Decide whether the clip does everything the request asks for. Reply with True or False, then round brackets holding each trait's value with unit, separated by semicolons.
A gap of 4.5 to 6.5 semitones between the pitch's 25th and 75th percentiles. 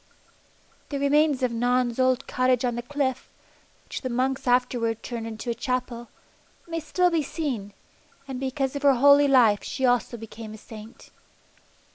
False (2.8 semitones)